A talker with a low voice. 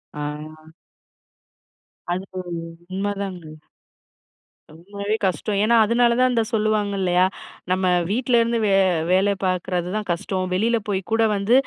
No: high, 195 Hz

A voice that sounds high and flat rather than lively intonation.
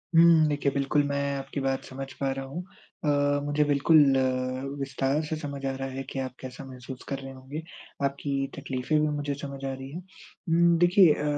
No: medium, 140 Hz; narrow, 1.9 semitones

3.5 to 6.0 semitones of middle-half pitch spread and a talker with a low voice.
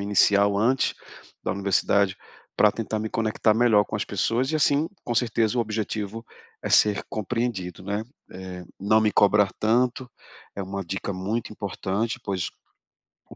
No: narrow, 2.6 semitones; low, 105 Hz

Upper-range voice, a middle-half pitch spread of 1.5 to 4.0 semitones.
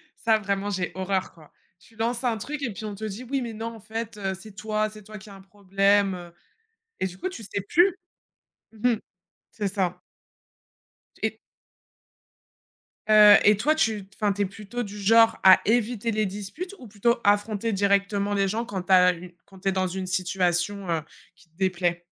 Yes: high, 205 Hz; average, 2.7 semitones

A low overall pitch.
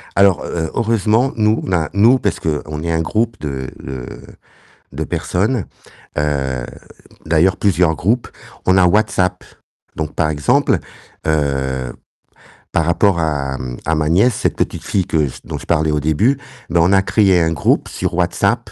Yes: very low, 85 Hz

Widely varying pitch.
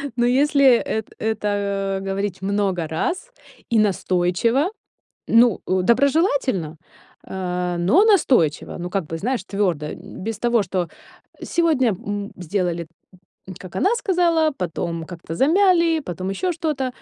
Yes: wide, 7.7 semitones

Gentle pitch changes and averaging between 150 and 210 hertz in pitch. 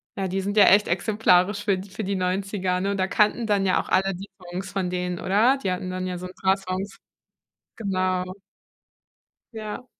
Yes: narrow, 1.7 semitones; high, 190 Hz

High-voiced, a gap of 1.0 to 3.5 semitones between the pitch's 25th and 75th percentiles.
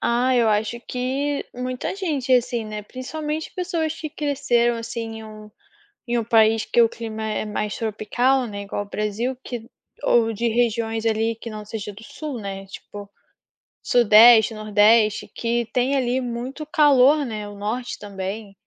Yes: high, 230 Hz; average, 3.0 semitones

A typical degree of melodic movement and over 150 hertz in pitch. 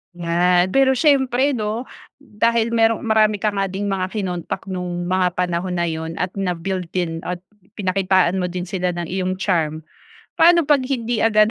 Yes: average, 4.0 semitones; high, 190 Hz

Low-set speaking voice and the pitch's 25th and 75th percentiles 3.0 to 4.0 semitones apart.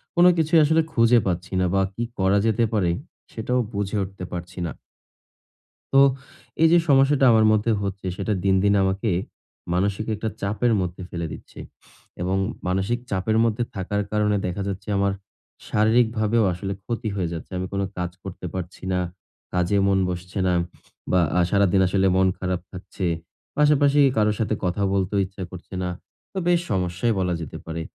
Yes: low, 100 Hz; average, 3.3 semitones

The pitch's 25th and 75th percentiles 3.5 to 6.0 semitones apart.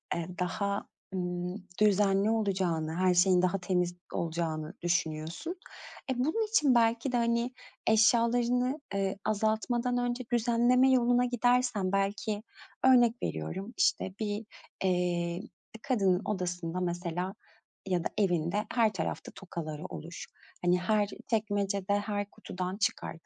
Yes: average, 4.7 semitones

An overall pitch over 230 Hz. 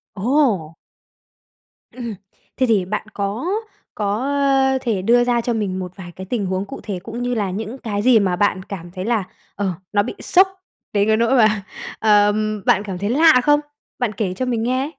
No: high, 215 Hz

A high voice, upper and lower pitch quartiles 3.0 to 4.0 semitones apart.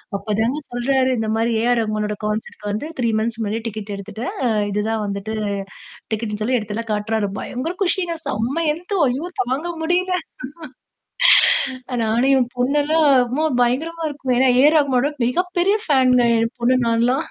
No: high, 245 Hz; average, 4.7 semitones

